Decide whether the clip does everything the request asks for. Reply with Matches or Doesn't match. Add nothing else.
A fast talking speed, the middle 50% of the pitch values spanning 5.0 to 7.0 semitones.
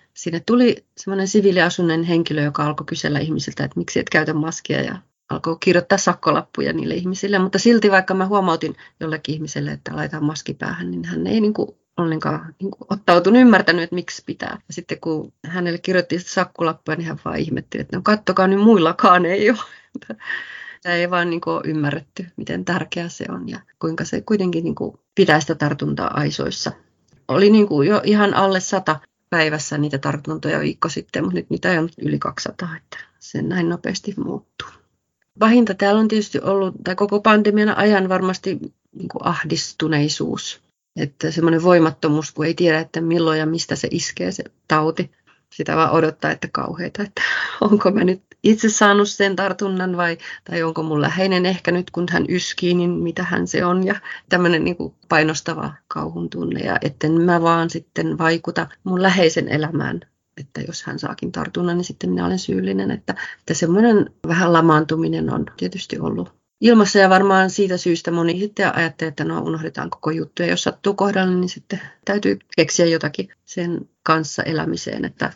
Doesn't match